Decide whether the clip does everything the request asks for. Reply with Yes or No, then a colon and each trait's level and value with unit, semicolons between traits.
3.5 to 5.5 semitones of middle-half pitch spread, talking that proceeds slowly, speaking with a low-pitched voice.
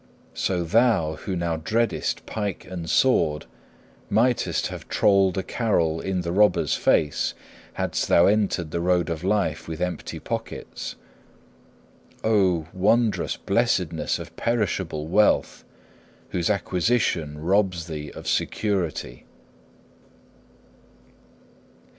Yes: average, 4.2 semitones; slow, 105 wpm; very low, 90 Hz